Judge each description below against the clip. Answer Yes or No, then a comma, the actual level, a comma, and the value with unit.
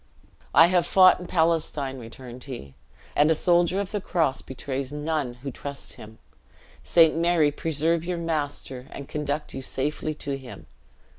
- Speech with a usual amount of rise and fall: Yes, average, 3.8 semitones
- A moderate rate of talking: Yes, average, 155 wpm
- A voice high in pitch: No, medium, 150 Hz